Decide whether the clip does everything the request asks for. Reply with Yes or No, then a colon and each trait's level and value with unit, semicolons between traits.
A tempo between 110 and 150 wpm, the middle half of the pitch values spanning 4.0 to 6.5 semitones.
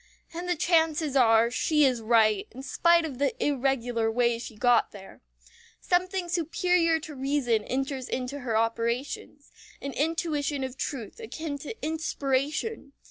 Yes: average, 140 wpm; average, 4.8 semitones